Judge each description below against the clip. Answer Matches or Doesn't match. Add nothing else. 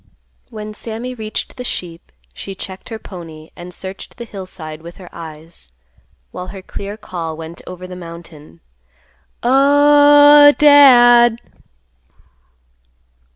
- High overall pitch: Matches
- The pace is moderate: Doesn't match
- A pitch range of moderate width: Doesn't match